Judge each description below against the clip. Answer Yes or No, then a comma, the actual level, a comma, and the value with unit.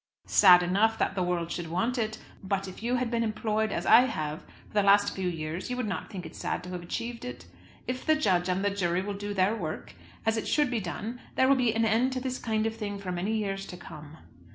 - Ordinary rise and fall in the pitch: Yes, average, 4.1 semitones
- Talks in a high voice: Yes, high, 205 Hz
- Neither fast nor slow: No, fast, 255 wpm